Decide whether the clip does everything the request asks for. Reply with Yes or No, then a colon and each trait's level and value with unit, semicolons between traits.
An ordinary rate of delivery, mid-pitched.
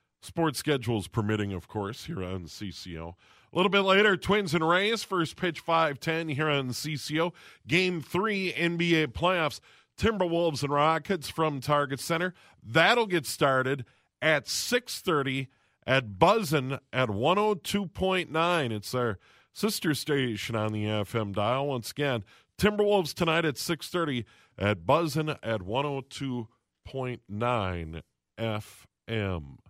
No: slow, 120 wpm; medium, 145 Hz